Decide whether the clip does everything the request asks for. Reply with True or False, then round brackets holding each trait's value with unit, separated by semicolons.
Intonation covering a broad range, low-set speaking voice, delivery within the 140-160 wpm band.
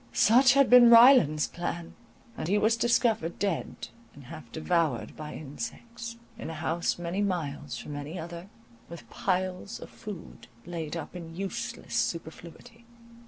False (5.7 semitones; 175 Hz; 145 wpm)